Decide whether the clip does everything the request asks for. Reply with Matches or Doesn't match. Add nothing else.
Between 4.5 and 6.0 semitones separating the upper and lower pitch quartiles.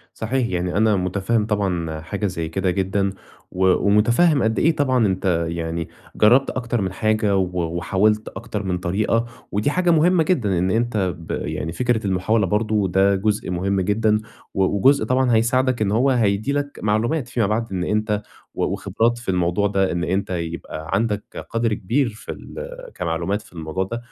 Doesn't match